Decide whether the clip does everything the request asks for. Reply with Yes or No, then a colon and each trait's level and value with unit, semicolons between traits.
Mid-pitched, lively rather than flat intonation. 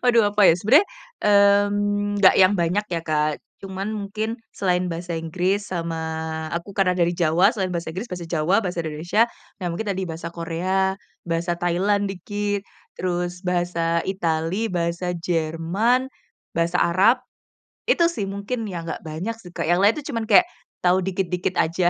No: medium, 180 Hz; average, 3.1 semitones